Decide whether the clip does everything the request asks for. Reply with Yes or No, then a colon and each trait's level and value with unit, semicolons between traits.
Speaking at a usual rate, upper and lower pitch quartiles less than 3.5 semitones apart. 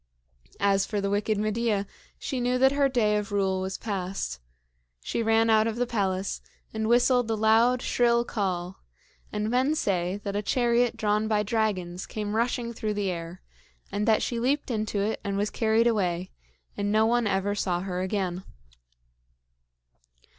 Yes: average, 170 wpm; average, 3.0 semitones